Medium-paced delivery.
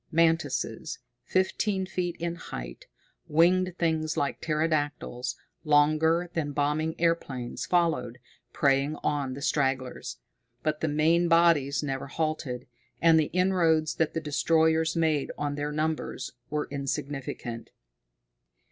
No: slow, 115 wpm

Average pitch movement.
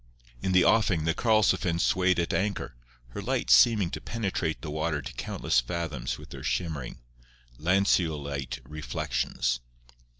Yes: average, 4.7 semitones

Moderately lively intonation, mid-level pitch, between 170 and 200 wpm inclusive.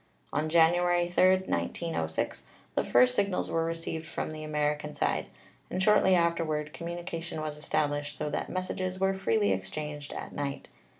No: average, 3.0 semitones; medium, 160 Hz; average, 155 wpm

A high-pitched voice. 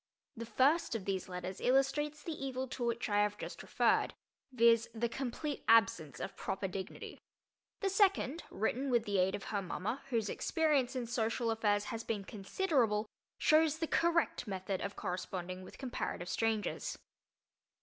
Yes: high, 230 Hz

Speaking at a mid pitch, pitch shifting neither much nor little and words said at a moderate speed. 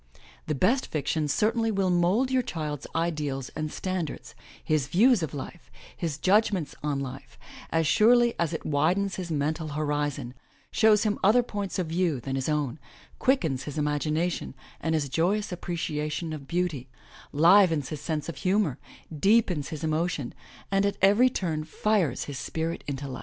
Yes: medium, 160 Hz; average, 4.7 semitones; average, 160 wpm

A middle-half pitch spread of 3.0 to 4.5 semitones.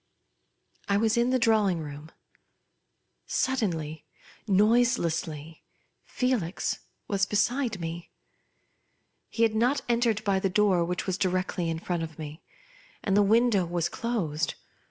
No: average, 5.3 semitones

